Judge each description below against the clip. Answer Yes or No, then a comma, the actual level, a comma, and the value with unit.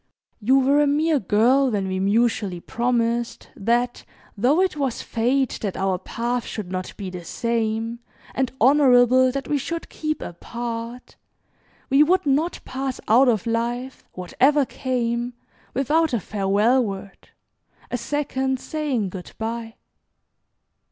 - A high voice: Yes, high, 240 Hz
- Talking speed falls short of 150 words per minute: Yes, slow, 135 wpm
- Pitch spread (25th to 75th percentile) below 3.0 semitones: No, average, 3.5 semitones